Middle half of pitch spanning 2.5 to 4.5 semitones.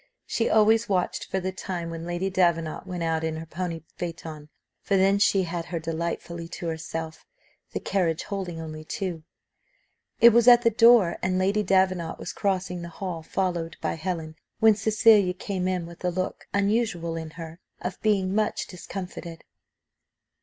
Yes: average, 3.0 semitones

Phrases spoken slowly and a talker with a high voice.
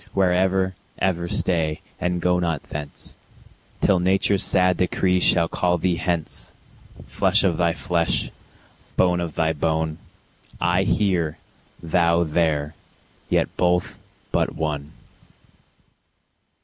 No: slow, 115 wpm; very low, 85 Hz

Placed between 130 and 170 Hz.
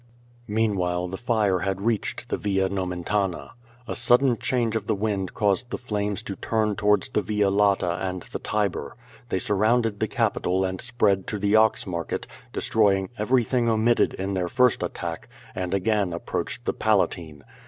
No: low, 100 Hz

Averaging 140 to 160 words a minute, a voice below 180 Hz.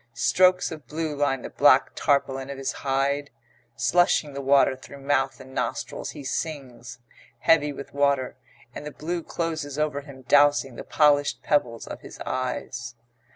Yes: average, 155 wpm; medium, 140 Hz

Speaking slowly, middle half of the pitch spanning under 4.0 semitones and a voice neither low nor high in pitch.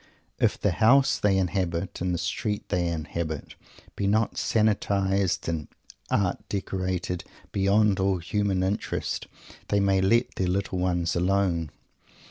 No: slow, 130 wpm; narrow, 2.4 semitones; very low, 95 Hz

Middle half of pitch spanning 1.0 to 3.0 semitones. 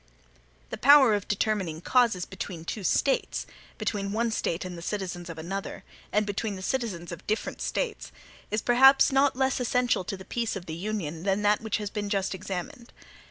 No: average, 4.2 semitones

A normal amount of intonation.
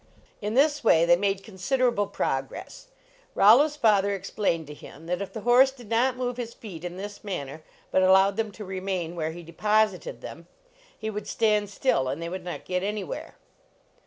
Yes: average, 4.2 semitones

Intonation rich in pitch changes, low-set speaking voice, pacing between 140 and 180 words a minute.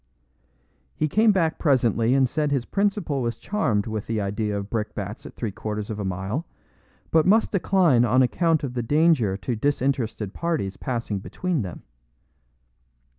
Yes: wide, 7.0 semitones; low, 125 Hz; average, 160 wpm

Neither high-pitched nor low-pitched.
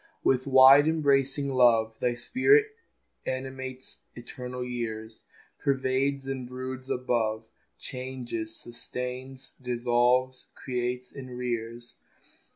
No: low, 125 Hz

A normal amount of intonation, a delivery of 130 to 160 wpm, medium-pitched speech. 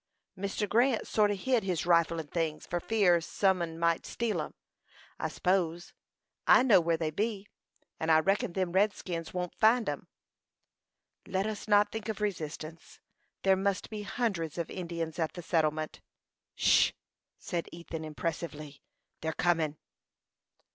Yes: average, 4.0 semitones; average, 150 wpm; medium, 175 Hz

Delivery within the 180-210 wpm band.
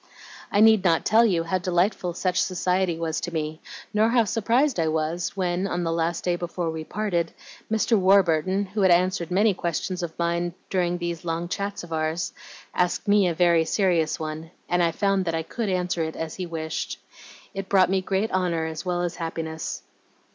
Yes: average, 195 wpm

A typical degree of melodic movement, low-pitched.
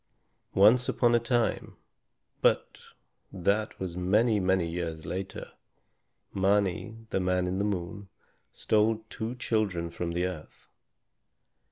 Yes: average, 3.4 semitones; very low, 95 Hz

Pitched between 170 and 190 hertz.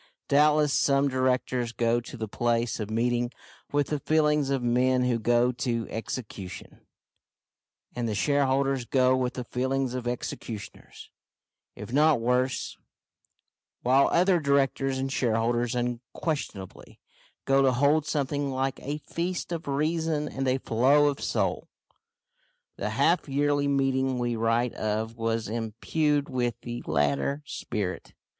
No: low, 130 Hz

